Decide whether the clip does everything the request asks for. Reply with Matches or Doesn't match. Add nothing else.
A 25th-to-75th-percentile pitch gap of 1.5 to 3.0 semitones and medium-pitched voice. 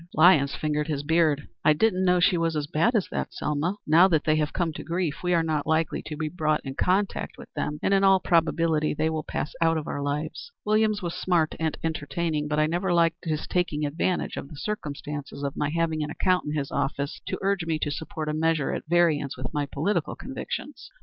Matches